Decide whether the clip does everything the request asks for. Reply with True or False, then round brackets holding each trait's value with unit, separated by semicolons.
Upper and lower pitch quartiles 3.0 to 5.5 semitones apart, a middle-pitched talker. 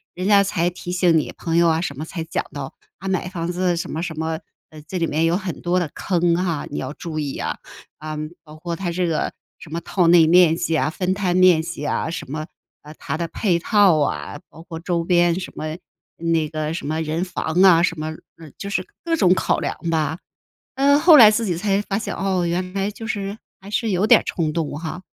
False (2.6 semitones; 170 Hz)